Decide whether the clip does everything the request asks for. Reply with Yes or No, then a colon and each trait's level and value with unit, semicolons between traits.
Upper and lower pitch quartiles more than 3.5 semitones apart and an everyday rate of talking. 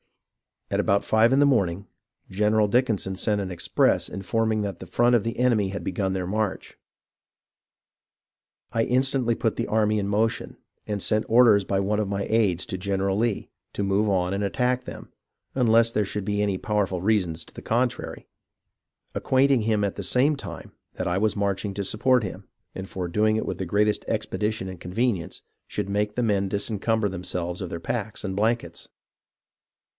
No: average, 2.7 semitones; average, 180 wpm